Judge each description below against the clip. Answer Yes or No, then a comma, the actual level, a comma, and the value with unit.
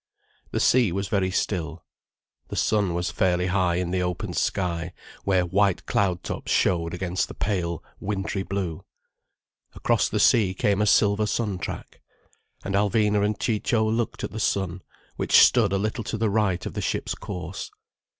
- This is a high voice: No, very low, 95 Hz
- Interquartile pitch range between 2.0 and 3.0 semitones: Yes, narrow, 2.6 semitones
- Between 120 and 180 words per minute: Yes, average, 170 wpm